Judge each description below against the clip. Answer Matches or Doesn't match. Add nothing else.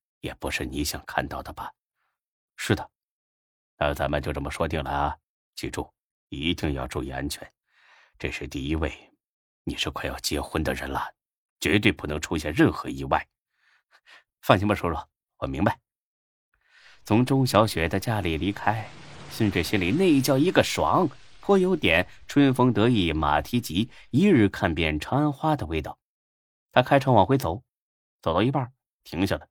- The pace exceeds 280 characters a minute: Doesn't match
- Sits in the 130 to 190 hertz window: Doesn't match